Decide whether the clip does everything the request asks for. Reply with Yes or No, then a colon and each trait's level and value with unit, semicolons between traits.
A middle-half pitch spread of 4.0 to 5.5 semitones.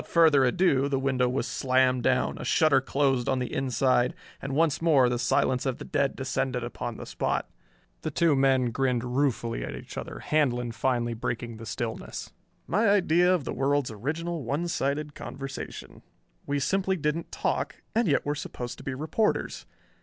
No: average, 3.5 semitones